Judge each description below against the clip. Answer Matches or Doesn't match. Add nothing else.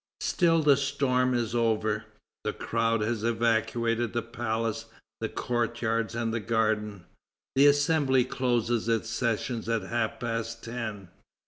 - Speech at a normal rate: Doesn't match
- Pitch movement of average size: Doesn't match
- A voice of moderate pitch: Doesn't match